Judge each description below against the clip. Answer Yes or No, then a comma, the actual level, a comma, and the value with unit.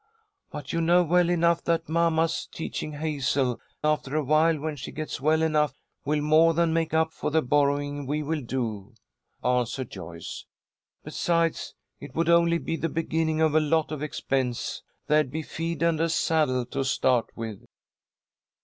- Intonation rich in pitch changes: No, average, 3.1 semitones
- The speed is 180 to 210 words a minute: No, average, 160 wpm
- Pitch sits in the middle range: Yes, medium, 155 Hz